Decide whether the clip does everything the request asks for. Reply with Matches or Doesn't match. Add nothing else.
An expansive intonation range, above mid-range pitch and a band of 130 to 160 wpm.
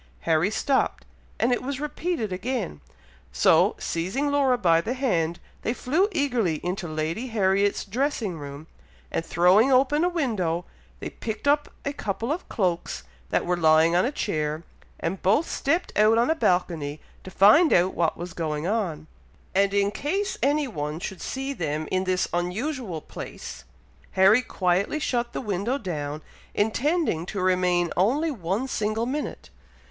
Matches